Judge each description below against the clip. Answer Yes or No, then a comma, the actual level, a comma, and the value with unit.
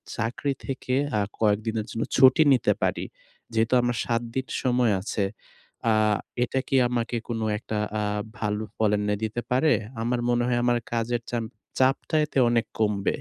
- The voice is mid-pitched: No, low, 120 Hz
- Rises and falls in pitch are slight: Yes, narrow, 2.2 semitones